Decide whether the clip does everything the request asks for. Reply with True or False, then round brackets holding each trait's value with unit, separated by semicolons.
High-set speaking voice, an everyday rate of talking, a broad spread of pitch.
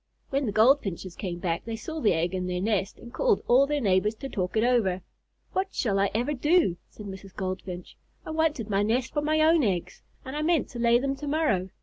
False (225 Hz; 230 wpm; 7.4 semitones)